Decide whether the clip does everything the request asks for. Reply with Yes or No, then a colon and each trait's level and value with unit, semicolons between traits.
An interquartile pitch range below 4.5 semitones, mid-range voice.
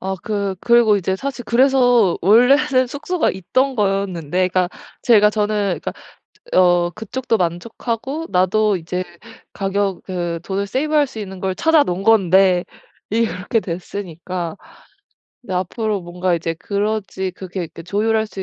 No: average, 3.9 semitones; high, 200 Hz